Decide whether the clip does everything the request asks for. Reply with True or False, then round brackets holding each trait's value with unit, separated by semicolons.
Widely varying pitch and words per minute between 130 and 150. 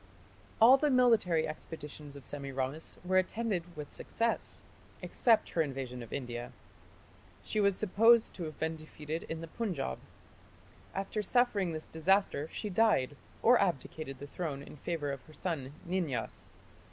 True (6.0 semitones; 145 wpm)